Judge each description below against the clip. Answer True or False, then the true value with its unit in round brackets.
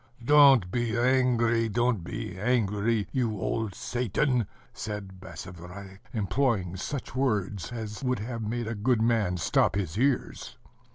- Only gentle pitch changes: False (3.9 semitones)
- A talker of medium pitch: False (110 Hz)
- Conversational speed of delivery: False (130 wpm)